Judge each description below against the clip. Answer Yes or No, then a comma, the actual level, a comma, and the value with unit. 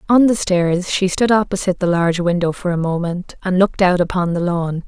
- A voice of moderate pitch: Yes, medium, 180 Hz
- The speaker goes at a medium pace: No, fast, 220 wpm